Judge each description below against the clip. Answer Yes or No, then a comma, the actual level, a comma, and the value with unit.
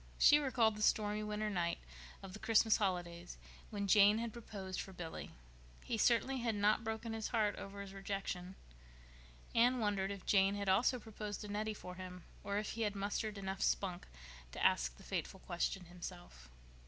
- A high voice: Yes, high, 205 Hz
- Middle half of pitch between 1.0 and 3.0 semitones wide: Yes, narrow, 2.5 semitones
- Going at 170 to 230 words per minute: Yes, average, 180 wpm